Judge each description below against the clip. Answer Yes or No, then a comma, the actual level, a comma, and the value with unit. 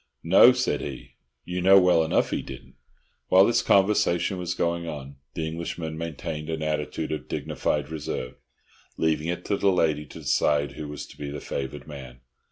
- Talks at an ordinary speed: Yes, average, 180 wpm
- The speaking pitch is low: Yes, very low, 80 Hz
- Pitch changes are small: No, average, 3.2 semitones